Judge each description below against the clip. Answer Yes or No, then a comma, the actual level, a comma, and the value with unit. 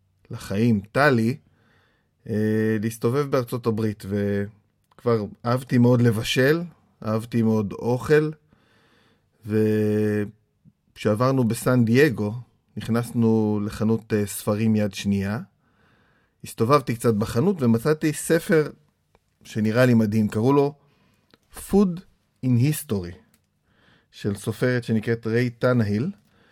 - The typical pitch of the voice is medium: No, low, 115 Hz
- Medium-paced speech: No, slow, 90 wpm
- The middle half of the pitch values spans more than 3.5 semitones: No, average, 3.0 semitones